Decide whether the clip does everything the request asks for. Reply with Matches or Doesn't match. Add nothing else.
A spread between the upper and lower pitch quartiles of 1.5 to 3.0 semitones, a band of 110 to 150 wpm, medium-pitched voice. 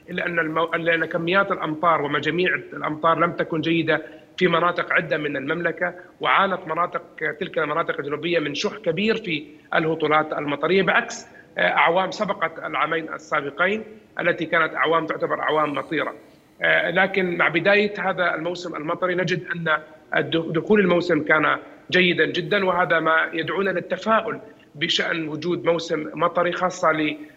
Matches